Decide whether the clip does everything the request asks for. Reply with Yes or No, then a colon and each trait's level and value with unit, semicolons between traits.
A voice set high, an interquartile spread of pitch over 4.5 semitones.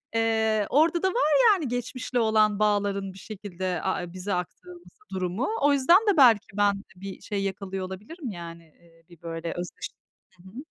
Yes: high, 205 Hz; average, 5.1 semitones